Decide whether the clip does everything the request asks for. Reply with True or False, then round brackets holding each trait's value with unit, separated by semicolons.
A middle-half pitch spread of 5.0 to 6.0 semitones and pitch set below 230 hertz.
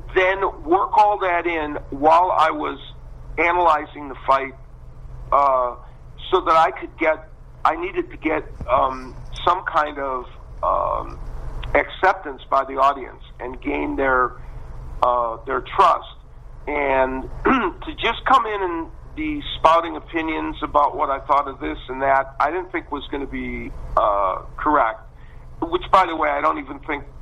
True (5.5 semitones; 135 Hz)